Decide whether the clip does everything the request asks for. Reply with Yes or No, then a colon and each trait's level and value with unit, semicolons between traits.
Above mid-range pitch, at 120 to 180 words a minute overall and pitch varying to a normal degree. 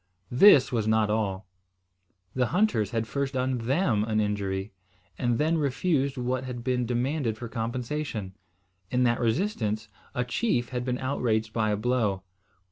No: low, 120 Hz; average, 150 wpm; average, 3.2 semitones